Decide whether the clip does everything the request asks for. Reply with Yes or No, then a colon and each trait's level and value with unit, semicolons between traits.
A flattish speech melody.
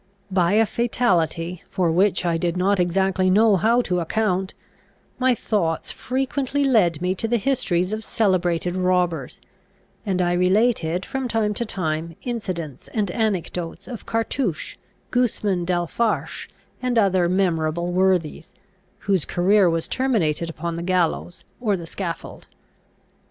No: average, 4.2 semitones